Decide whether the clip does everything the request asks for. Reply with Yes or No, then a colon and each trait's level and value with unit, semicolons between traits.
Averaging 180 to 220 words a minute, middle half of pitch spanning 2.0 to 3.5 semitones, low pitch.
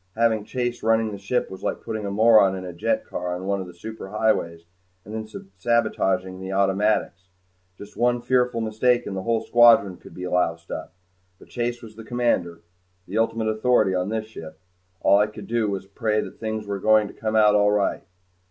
Yes: average, 200 wpm; average, 2.9 semitones; low, 105 Hz